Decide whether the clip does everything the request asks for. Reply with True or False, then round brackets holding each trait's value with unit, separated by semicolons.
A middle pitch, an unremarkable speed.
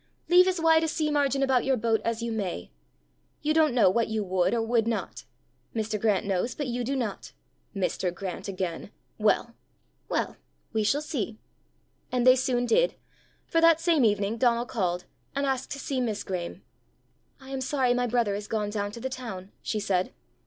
False (235 Hz; 190 wpm)